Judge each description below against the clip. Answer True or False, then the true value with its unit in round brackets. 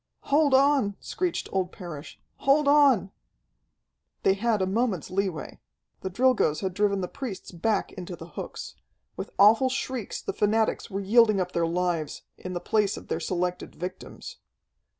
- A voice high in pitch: True (200 Hz)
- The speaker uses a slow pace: False (155 wpm)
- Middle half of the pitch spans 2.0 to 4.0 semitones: False (4.8 semitones)